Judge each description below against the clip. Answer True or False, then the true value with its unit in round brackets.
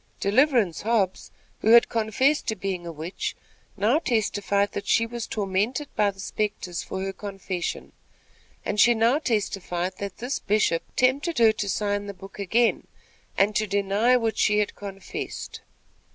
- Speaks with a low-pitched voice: False (205 Hz)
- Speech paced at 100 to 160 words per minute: True (155 wpm)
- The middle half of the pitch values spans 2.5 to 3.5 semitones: True (3.1 semitones)